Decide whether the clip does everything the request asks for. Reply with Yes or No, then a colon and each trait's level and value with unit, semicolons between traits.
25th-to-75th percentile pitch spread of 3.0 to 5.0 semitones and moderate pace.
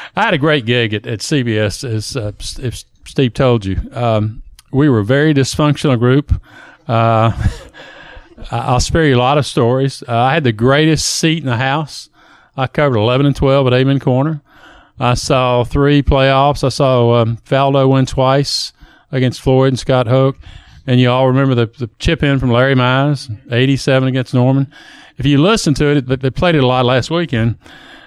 No: narrow, 2.6 semitones; average, 185 wpm